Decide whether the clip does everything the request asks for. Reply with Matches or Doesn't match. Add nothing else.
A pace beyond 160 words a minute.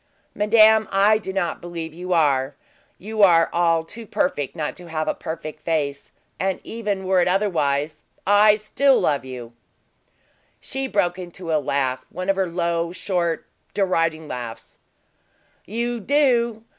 Doesn't match